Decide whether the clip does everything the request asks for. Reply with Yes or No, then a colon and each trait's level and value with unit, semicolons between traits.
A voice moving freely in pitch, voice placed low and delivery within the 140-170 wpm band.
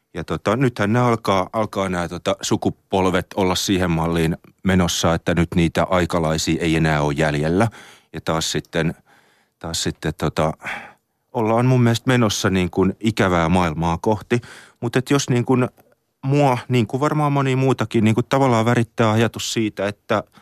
Yes: wide, 5.9 semitones; low, 100 Hz; fast, 155 wpm